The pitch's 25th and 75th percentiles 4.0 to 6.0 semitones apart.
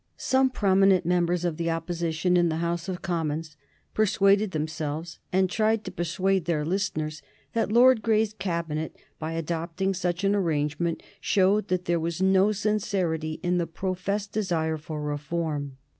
No: average, 3.3 semitones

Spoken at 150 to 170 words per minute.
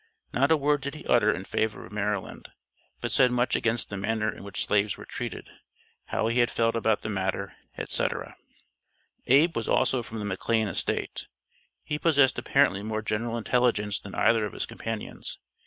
No: average, 180 wpm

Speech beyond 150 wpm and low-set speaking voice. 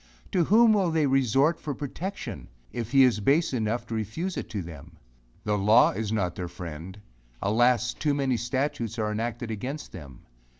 Yes: average, 175 wpm; low, 120 Hz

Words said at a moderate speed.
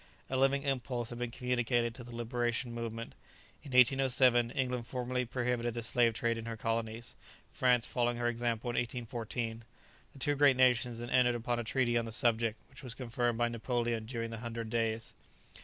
Yes: average, 185 wpm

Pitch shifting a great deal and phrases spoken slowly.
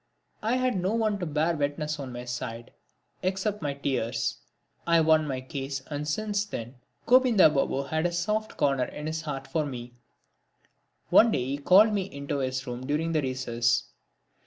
No: wide, 5.9 semitones; average, 175 wpm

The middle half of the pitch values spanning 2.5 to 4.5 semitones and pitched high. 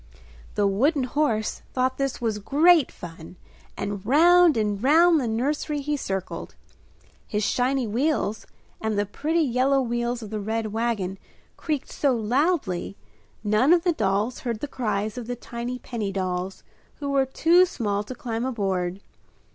No: average, 5.2 semitones; high, 240 Hz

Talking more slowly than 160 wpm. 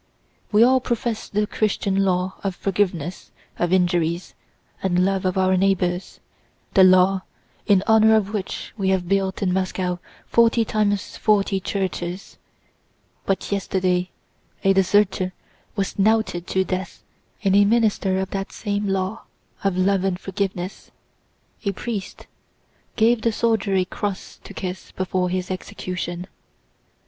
Yes: slow, 135 wpm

